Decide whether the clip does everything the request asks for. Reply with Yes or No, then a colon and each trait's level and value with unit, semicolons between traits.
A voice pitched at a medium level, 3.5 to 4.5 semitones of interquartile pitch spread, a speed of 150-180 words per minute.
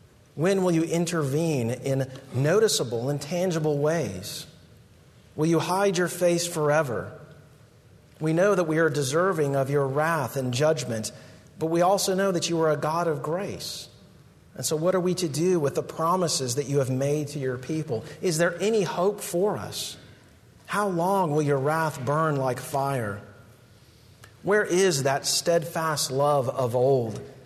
Yes: medium, 155 Hz; average, 4.2 semitones; average, 165 wpm